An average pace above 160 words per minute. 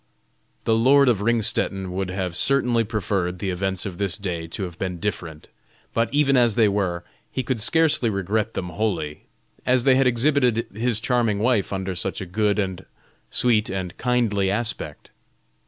Yes: average, 170 wpm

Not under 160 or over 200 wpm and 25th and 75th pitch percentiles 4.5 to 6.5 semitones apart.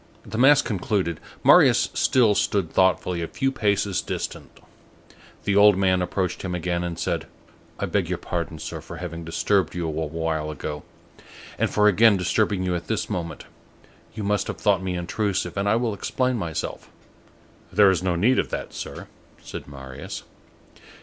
No: average, 170 wpm; average, 3.5 semitones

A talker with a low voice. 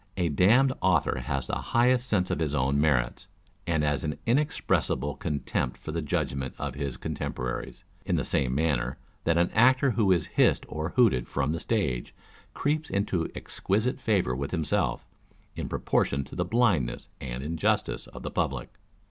Yes: very low, 80 Hz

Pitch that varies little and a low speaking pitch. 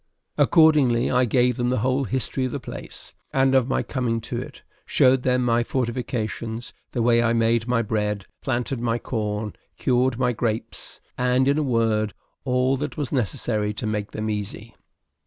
Yes: narrow, 2.3 semitones; low, 120 Hz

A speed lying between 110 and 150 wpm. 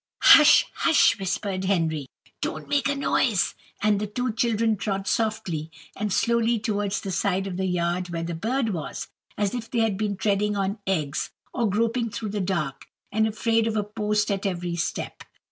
No: average, 180 wpm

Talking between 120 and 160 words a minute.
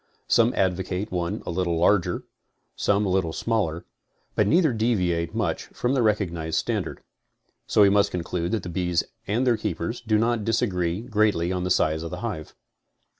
No: average, 175 wpm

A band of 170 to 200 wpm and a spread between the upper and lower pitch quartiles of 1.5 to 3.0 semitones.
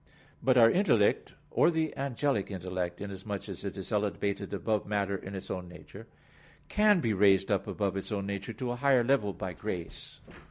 No: average, 185 wpm; average, 3.9 semitones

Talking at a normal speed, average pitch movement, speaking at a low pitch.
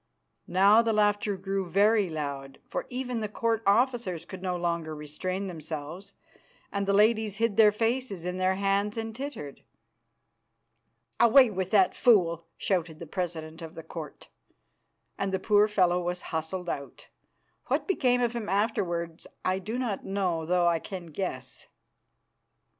No: average, 150 wpm; average, 4.0 semitones; high, 190 Hz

